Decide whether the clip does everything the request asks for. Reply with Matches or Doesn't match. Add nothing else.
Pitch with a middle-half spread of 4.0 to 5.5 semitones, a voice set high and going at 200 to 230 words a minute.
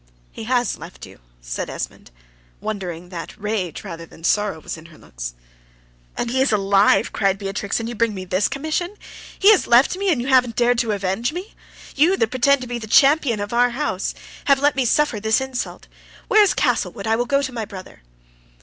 Matches